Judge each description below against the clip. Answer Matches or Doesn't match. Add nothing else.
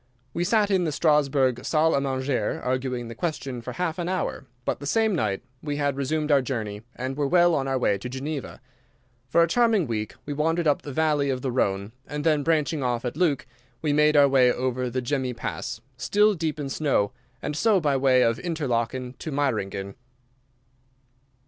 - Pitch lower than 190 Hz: Matches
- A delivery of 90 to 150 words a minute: Doesn't match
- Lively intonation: Doesn't match